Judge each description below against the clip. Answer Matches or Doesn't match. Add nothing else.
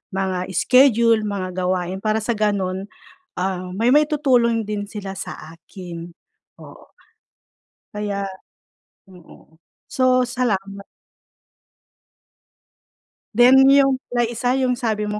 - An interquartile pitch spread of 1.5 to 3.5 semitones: Doesn't match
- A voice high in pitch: Matches